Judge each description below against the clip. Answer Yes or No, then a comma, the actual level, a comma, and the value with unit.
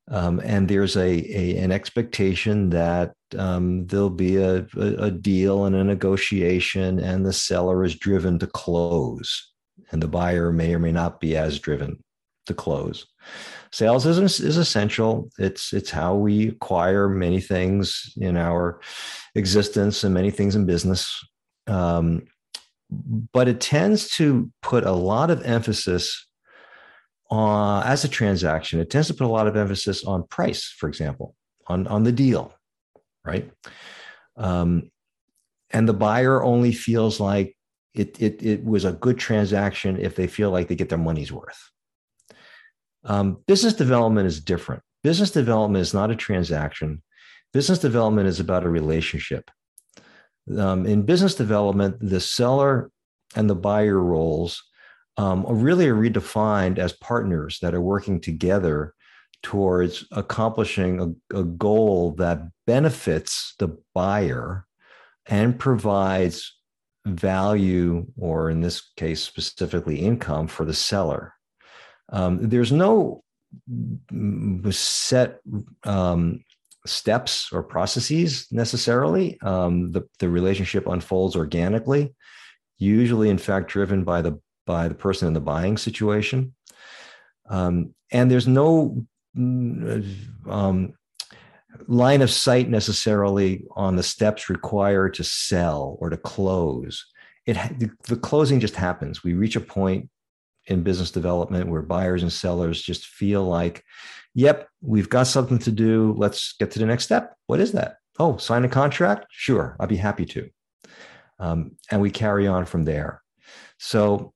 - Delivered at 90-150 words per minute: Yes, average, 140 wpm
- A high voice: No, low, 100 Hz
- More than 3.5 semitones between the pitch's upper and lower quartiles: Yes, average, 4.1 semitones